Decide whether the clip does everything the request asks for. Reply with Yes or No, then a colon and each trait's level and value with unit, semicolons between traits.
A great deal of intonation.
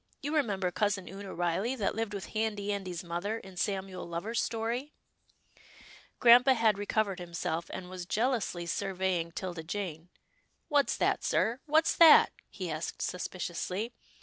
No: average, 4.0 semitones